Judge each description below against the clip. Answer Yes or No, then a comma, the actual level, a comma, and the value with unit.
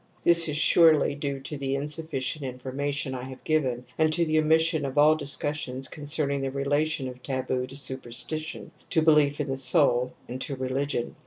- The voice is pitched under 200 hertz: Yes, medium, 140 Hz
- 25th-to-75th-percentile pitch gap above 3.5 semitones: No, average, 2.9 semitones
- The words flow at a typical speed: Yes, average, 185 wpm